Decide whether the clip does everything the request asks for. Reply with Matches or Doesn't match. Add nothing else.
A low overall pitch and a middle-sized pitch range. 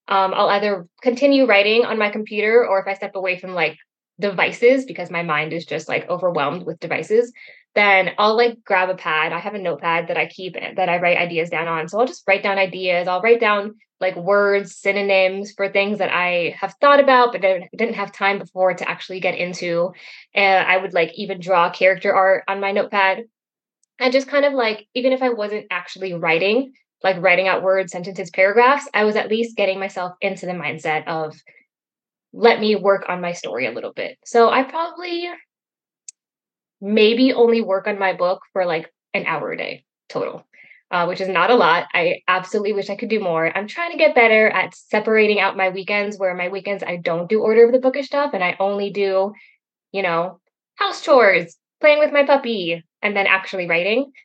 Doesn't match